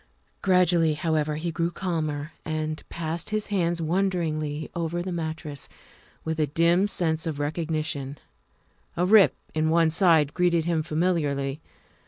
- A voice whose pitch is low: No, medium, 160 Hz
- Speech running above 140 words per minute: No, slow, 135 wpm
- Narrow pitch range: Yes, narrow, 2.0 semitones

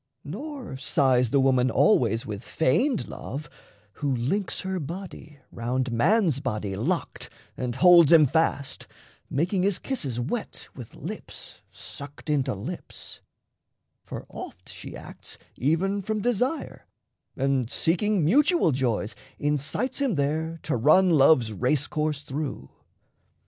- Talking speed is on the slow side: Yes, slow, 125 wpm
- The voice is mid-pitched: Yes, medium, 150 Hz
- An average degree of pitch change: No, wide, 6.5 semitones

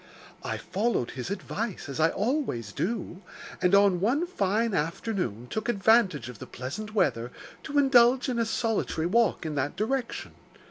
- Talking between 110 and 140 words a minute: No, average, 155 wpm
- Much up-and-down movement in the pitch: Yes, wide, 6.8 semitones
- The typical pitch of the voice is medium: No, high, 200 Hz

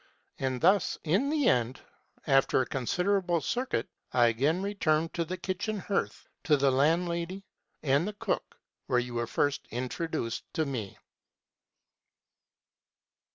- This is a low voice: No, medium, 155 Hz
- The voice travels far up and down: Yes, wide, 6.2 semitones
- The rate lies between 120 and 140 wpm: Yes, slow, 135 wpm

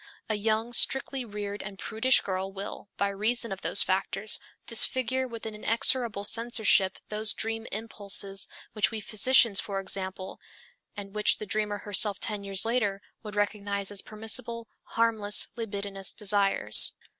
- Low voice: No, high, 210 Hz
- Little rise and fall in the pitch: Yes, narrow, 2.2 semitones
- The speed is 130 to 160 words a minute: Yes, average, 145 wpm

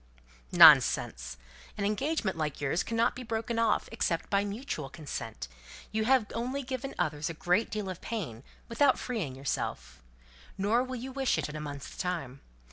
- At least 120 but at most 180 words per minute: Yes, average, 160 wpm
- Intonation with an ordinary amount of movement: No, wide, 8.0 semitones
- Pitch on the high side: Yes, high, 200 Hz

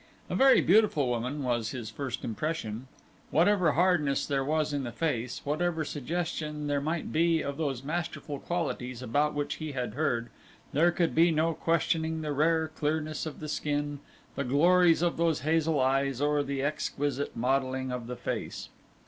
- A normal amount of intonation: Yes, average, 3.2 semitones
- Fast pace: No, average, 165 wpm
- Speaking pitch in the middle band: Yes, medium, 150 Hz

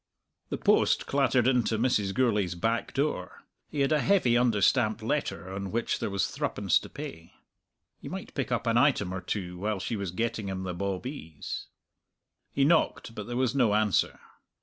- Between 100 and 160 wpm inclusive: No, average, 185 wpm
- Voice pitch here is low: Yes, low, 110 Hz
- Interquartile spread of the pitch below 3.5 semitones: No, average, 4.8 semitones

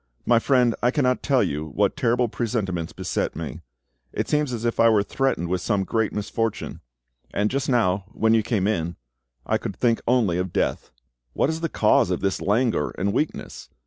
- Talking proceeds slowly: No, average, 190 wpm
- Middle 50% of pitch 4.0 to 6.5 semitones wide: Yes, average, 4.4 semitones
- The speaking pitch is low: Yes, low, 115 Hz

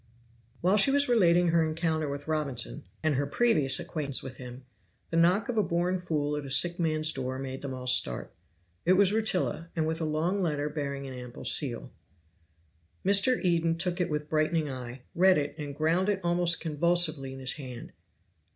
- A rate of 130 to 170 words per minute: No, average, 185 wpm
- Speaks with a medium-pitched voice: Yes, medium, 155 Hz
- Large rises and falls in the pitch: No, average, 4.0 semitones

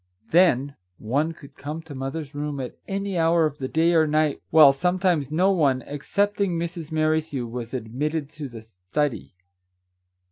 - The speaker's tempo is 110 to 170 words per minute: Yes, average, 155 wpm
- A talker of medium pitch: Yes, medium, 150 Hz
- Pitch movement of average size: Yes, average, 3.4 semitones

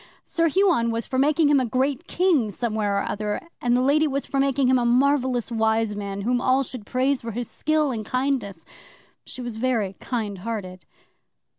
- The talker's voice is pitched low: No, high, 245 Hz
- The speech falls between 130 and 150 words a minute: No, average, 190 wpm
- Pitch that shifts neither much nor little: Yes, average, 3.9 semitones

